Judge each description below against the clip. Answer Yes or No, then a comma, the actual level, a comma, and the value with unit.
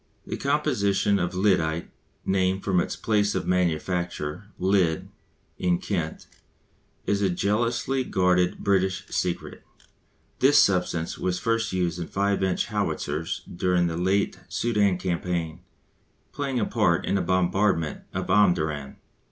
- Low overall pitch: Yes, very low, 95 Hz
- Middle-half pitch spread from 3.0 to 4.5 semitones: No, narrow, 2.6 semitones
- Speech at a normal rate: No, slow, 125 wpm